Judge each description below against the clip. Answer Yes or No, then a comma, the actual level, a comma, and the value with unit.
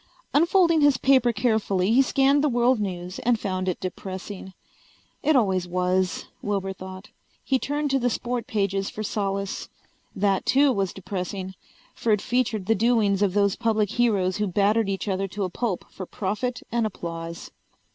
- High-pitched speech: Yes, high, 205 Hz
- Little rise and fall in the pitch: No, average, 4.3 semitones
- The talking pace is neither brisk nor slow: Yes, average, 165 wpm